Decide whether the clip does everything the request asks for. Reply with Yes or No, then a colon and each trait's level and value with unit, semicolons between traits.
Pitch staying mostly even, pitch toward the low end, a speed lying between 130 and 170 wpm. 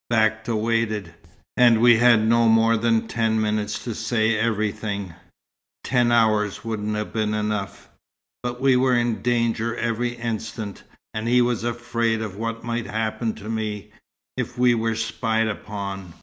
Yes: narrow, 1.6 semitones; low, 115 Hz; average, 150 wpm